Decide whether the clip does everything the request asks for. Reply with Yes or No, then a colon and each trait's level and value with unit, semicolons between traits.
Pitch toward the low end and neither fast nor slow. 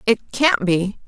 No: high, 210 Hz; average, 170 wpm